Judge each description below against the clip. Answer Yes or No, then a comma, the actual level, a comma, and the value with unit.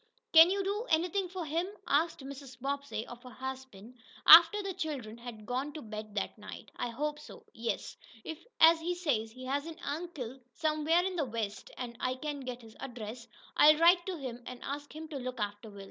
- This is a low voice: No, very high, 280 Hz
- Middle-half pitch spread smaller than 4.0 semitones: No, average, 5.1 semitones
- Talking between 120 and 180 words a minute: No, fast, 205 wpm